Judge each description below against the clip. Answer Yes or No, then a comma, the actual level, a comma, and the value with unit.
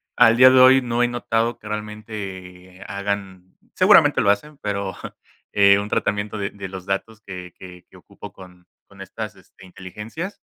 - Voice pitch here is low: Yes, low, 100 Hz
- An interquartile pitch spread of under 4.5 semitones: Yes, average, 3.1 semitones